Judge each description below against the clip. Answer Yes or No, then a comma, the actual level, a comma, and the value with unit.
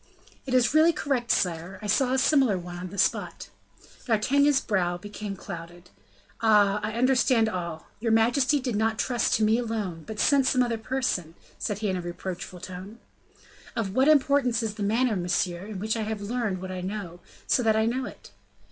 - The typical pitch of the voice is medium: No, high, 215 Hz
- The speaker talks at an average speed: Yes, average, 190 wpm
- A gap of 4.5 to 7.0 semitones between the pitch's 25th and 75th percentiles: Yes, average, 5.0 semitones